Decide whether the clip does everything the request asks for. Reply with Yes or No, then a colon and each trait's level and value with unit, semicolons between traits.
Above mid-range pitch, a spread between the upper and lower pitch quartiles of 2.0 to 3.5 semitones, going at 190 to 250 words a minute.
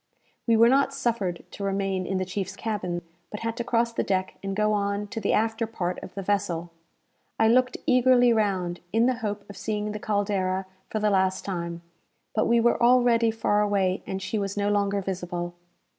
Yes: high, 205 Hz; average, 3.1 semitones; average, 200 wpm